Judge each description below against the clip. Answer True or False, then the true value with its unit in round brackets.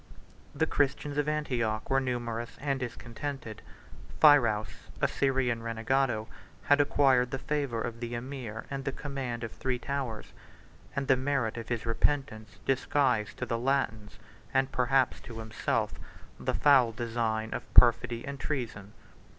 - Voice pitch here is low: True (125 Hz)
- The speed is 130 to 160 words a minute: True (140 wpm)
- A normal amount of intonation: True (3.1 semitones)